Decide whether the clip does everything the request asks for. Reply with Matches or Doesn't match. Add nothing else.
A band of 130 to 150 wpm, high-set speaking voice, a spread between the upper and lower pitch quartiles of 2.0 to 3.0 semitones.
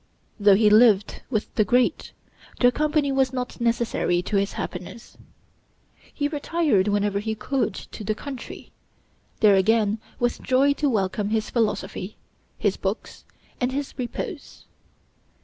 Doesn't match